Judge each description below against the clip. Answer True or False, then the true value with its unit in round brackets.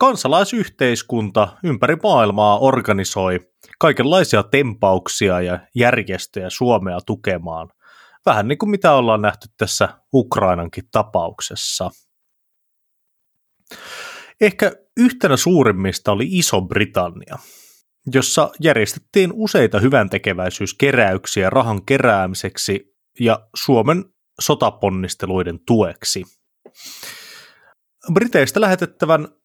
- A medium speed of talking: False (75 wpm)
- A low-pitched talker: True (120 Hz)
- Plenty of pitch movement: True (9.0 semitones)